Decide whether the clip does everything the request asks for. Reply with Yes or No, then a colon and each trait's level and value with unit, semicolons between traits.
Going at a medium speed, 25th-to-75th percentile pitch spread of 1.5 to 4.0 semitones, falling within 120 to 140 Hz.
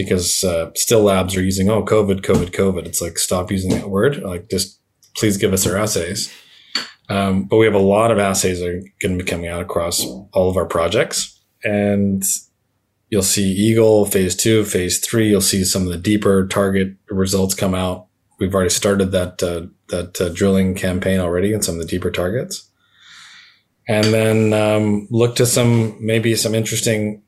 No: average, 190 wpm; narrow, 2.4 semitones; low, 100 Hz